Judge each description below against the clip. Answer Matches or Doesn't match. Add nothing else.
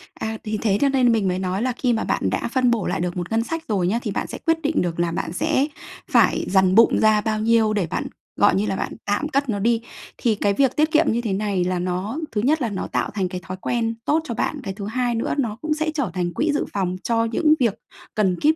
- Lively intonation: Doesn't match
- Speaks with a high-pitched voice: Matches